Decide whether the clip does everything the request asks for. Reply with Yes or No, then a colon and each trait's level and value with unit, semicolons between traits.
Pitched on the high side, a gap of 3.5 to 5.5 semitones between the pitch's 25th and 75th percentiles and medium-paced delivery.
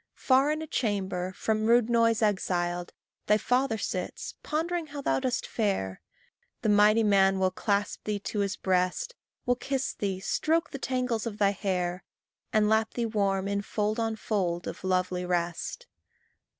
Yes: high, 210 Hz; average, 4.1 semitones; average, 165 wpm